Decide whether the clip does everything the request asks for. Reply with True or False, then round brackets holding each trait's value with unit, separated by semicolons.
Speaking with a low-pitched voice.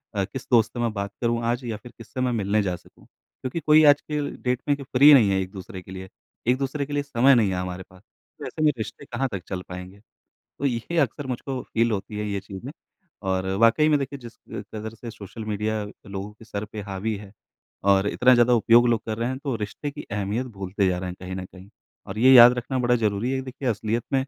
True (115 Hz)